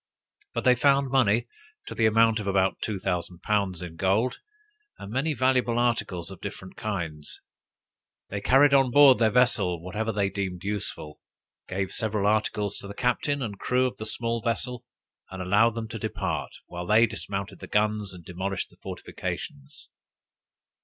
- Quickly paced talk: No, average, 165 wpm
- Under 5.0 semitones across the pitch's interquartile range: Yes, average, 3.7 semitones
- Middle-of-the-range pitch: No, low, 105 Hz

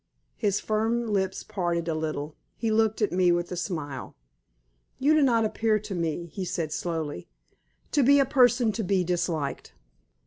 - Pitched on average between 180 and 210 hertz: Yes, high, 190 Hz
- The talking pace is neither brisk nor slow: Yes, average, 170 wpm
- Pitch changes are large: No, average, 4.8 semitones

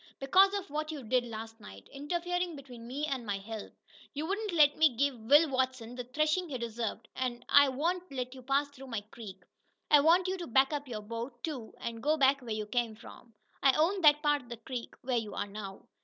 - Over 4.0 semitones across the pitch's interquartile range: Yes, average, 4.6 semitones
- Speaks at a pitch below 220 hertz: No, very high, 265 Hz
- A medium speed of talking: No, fast, 225 wpm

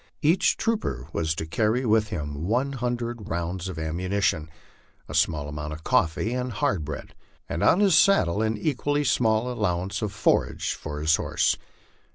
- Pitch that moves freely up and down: Yes, wide, 7.2 semitones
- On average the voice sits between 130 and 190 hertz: No, low, 105 Hz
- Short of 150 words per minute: No, average, 165 wpm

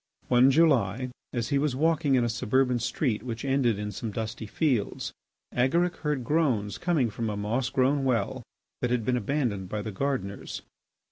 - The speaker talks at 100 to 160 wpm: No, average, 175 wpm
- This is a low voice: Yes, low, 125 Hz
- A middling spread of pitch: Yes, average, 3.9 semitones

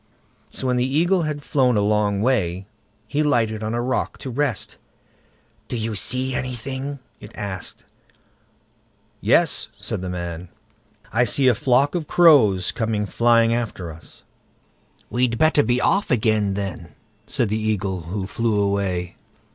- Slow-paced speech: No, average, 145 wpm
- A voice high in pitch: No, low, 115 Hz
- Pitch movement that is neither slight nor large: Yes, average, 4.4 semitones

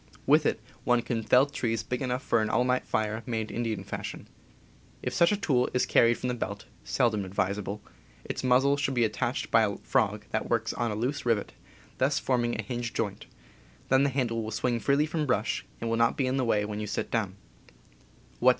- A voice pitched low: Yes, low, 120 Hz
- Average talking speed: No, fast, 210 wpm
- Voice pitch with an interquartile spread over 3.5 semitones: No, average, 2.8 semitones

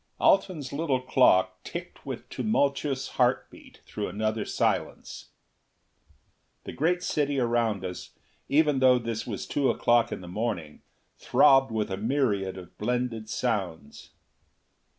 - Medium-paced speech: No, slow, 125 wpm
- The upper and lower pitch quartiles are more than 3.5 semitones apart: Yes, average, 4.8 semitones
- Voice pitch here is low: Yes, low, 120 Hz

